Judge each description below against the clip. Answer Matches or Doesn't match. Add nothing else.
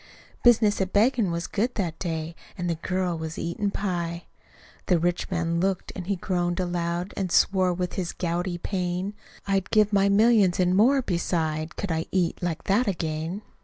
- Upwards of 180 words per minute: Doesn't match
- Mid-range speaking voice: Matches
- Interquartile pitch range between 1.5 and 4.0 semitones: Matches